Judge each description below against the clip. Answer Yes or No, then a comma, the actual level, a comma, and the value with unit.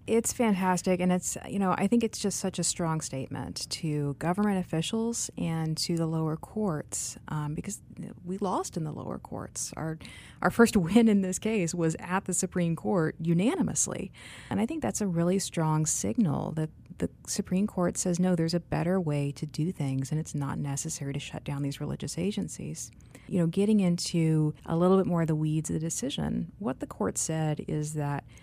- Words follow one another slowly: No, average, 200 wpm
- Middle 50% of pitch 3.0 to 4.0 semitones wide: Yes, average, 3.6 semitones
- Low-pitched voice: No, medium, 170 Hz